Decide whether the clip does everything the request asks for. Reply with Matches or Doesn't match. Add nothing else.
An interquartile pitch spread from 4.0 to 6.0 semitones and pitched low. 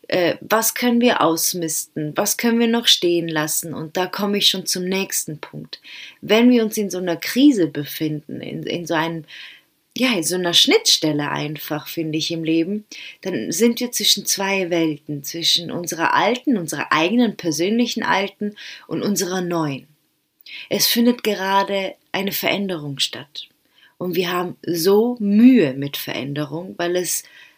Doesn't match